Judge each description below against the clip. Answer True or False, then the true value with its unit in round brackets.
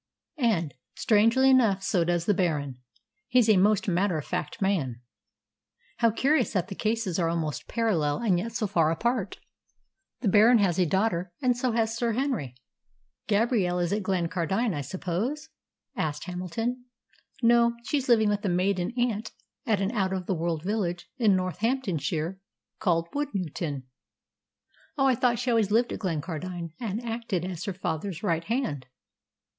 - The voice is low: False (195 Hz)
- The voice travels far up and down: False (5.0 semitones)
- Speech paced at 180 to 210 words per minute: False (160 wpm)